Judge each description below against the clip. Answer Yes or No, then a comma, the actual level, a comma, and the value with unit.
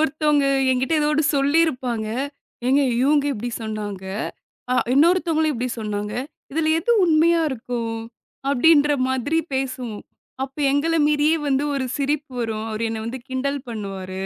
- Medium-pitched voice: No, very high, 270 Hz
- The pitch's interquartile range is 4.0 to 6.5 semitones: Yes, average, 4.8 semitones